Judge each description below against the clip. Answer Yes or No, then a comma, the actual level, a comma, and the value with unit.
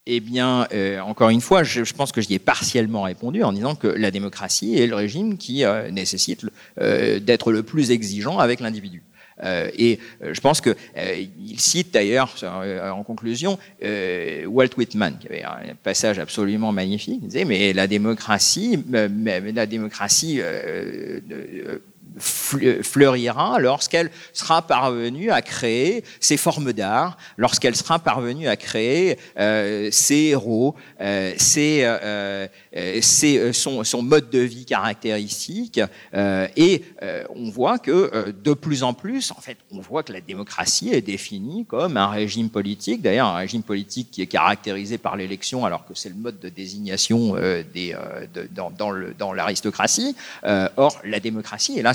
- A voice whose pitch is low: Yes, low, 115 Hz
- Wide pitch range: Yes, wide, 6.1 semitones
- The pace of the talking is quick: No, average, 155 wpm